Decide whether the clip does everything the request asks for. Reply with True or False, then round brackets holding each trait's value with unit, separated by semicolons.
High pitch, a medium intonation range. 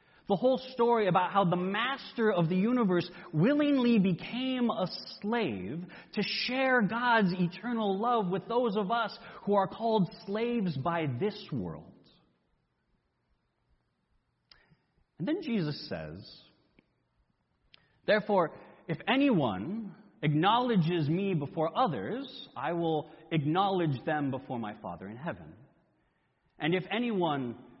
False (195 Hz; 6.0 semitones)